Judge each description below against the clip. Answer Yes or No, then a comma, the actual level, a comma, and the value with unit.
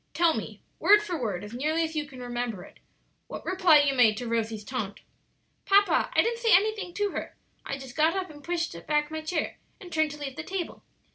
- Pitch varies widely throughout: Yes, wide, 6.2 semitones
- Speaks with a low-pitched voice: No, very high, 310 Hz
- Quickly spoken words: Yes, fast, 220 wpm